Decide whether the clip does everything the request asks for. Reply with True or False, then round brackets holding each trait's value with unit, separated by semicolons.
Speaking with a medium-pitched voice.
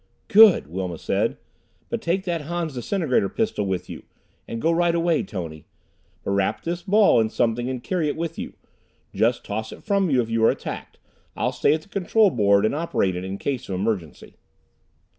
False (130 Hz)